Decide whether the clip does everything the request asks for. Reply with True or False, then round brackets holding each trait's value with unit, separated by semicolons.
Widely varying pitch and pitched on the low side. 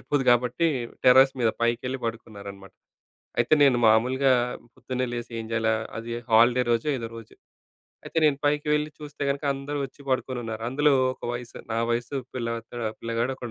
False (2.8 semitones; 120 Hz)